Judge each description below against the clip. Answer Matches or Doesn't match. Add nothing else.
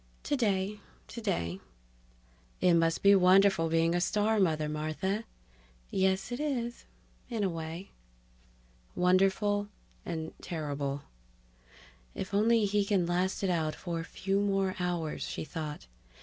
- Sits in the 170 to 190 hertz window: Matches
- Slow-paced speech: Matches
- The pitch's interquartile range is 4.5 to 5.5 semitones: Doesn't match